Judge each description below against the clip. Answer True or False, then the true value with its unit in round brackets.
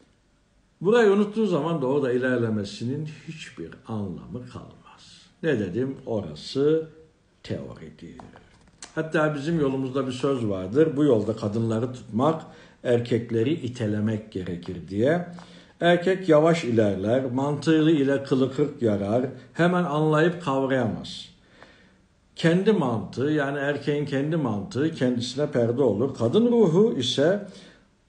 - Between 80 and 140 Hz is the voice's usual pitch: True (135 Hz)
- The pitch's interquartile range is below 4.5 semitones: False (5.5 semitones)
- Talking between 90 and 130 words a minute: True (105 wpm)